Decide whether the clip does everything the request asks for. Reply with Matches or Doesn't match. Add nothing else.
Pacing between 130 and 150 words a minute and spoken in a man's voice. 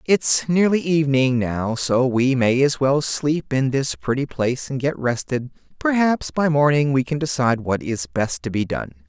Doesn't match